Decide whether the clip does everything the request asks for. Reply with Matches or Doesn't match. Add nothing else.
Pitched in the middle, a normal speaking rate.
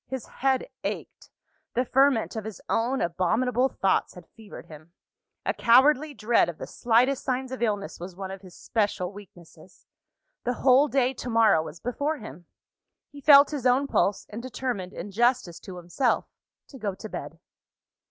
Doesn't match